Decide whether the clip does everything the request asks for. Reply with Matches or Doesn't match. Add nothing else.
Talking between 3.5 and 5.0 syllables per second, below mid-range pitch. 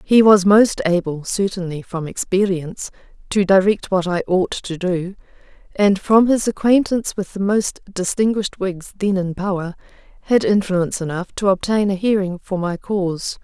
Doesn't match